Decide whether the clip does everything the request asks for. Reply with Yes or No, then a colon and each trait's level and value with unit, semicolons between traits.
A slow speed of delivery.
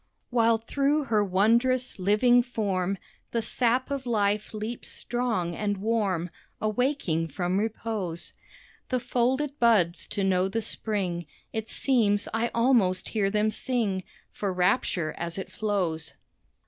Yes: slow, 130 wpm